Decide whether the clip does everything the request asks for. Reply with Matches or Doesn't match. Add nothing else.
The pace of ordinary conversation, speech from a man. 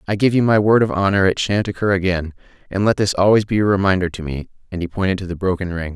Doesn't match